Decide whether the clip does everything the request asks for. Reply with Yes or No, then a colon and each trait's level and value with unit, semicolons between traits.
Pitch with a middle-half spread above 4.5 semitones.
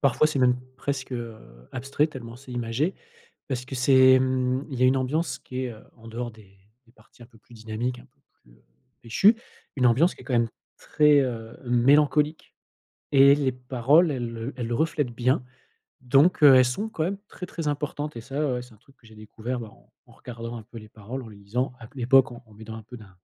No: average, 3.1 semitones